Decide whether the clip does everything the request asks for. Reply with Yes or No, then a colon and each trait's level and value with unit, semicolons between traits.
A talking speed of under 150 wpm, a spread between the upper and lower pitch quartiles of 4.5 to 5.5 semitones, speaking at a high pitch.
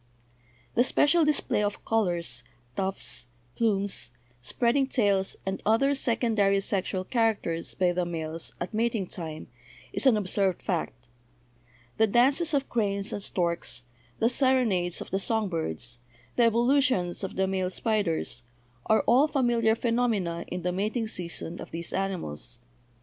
Yes: average, 140 wpm; average, 4.9 semitones; high, 200 Hz